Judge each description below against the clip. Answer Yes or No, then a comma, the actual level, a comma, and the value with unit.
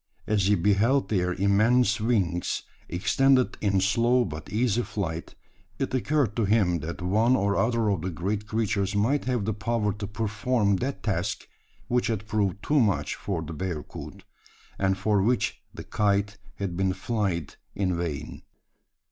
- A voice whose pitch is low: Yes, low, 105 Hz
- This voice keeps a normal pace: Yes, average, 155 wpm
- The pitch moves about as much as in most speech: Yes, average, 3.4 semitones